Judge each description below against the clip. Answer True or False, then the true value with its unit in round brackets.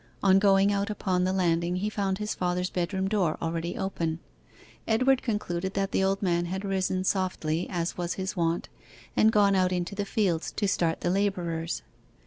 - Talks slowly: False (180 wpm)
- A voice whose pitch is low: False (190 Hz)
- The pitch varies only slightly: True (2.3 semitones)